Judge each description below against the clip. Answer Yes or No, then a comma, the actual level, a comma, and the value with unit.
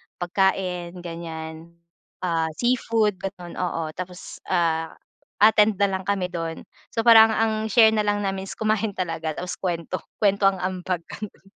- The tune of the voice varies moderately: Yes, average, 3.5 semitones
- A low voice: No, medium, 185 Hz